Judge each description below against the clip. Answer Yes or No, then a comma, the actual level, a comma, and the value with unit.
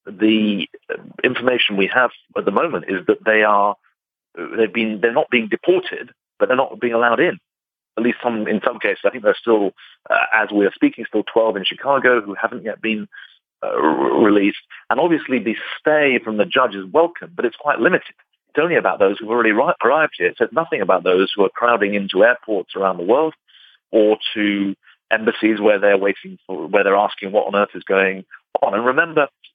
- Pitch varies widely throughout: Yes, wide, 6.4 semitones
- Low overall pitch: Yes, low, 115 Hz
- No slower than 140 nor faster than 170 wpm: No, fast, 205 wpm